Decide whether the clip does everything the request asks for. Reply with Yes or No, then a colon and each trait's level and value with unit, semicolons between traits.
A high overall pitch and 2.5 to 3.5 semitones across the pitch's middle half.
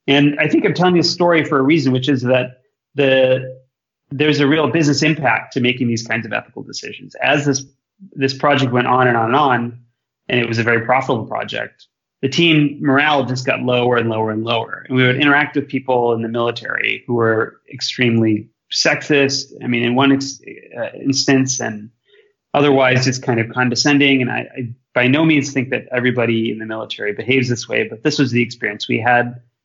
No: low, 130 Hz; average, 3.0 semitones